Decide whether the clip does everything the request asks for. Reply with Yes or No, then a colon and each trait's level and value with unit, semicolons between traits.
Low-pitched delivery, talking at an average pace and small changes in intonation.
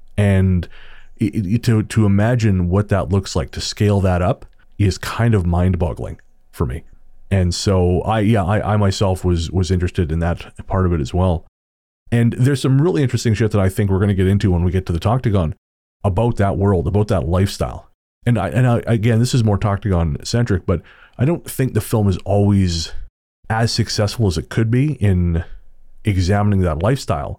No: low, 100 Hz; average, 190 wpm; average, 3.7 semitones